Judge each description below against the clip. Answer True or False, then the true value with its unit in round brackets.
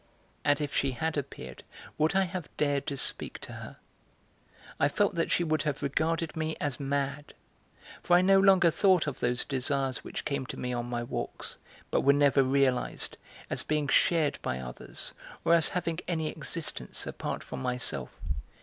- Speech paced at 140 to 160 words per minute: False (175 wpm)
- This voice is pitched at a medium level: True (145 Hz)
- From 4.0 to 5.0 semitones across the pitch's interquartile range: False (3.4 semitones)